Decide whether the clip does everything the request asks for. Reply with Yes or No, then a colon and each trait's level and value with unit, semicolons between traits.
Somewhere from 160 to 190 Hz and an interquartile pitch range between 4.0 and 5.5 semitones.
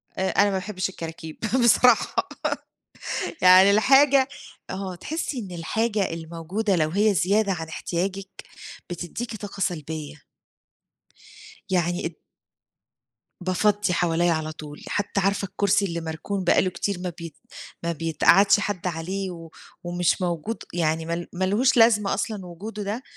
No: medium, 185 Hz; average, 3.5 semitones